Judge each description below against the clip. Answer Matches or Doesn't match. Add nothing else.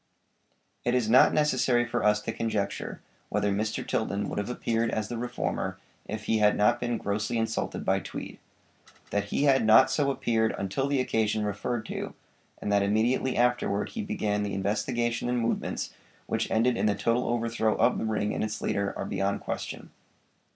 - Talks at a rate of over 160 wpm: Matches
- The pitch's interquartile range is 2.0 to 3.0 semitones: Matches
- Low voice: Matches